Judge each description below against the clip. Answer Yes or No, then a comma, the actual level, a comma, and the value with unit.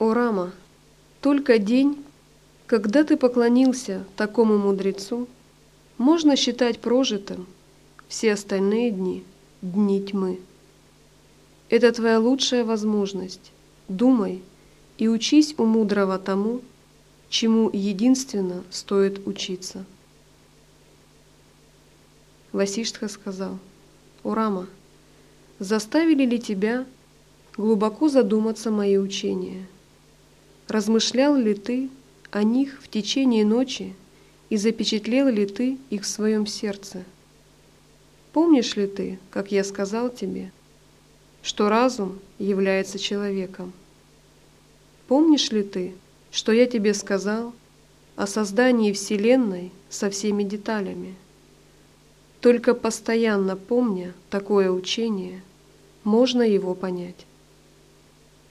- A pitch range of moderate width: Yes, average, 3.6 semitones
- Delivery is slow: Yes, slow, 90 wpm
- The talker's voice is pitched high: Yes, high, 210 Hz